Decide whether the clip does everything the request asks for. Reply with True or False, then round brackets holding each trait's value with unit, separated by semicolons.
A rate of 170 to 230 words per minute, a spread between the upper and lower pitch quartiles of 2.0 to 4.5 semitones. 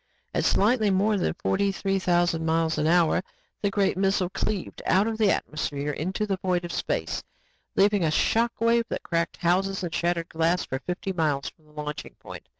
True (180 wpm; 3.4 semitones)